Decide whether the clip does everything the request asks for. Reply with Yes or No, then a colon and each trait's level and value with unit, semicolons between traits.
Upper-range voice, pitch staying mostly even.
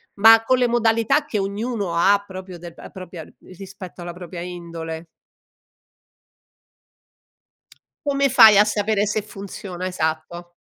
No: high, 195 Hz; average, 3.9 semitones